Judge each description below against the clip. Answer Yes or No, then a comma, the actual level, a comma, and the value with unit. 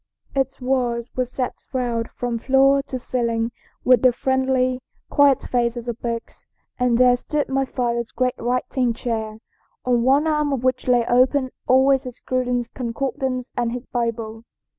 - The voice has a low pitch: No, very high, 250 Hz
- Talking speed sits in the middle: Yes, average, 155 wpm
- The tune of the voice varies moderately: No, narrow, 1.8 semitones